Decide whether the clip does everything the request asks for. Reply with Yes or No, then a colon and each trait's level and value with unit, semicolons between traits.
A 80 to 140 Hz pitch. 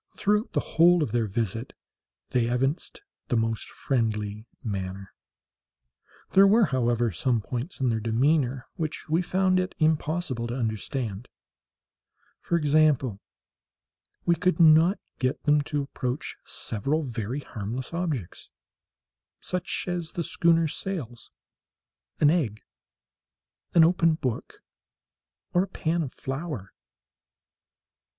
Yes: low, 135 Hz